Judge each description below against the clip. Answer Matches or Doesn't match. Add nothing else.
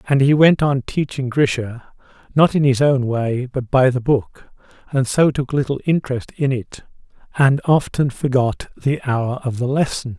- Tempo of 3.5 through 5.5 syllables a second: Matches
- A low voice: Matches